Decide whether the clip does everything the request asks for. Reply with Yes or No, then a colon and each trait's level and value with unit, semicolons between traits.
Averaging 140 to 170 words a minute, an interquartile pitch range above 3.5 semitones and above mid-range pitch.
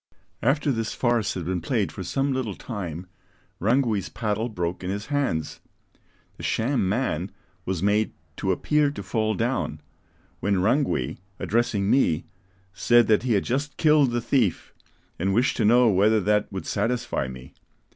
No: average, 155 wpm; average, 4.7 semitones; low, 110 Hz